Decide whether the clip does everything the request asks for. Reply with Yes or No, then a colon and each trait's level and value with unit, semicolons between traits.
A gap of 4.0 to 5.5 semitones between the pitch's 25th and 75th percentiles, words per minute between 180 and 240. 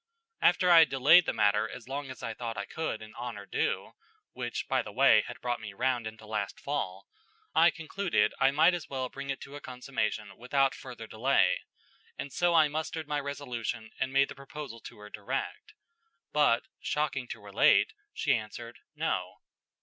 Yes: average, 4.7 semitones; average, 185 wpm